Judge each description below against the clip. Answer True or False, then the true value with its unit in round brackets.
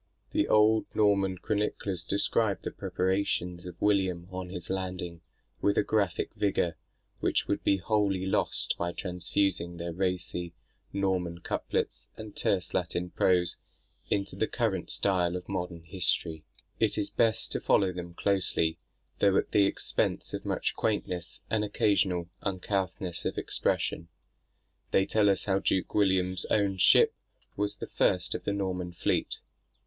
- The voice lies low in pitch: True (95 Hz)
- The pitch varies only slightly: True (2.3 semitones)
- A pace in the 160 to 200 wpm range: False (145 wpm)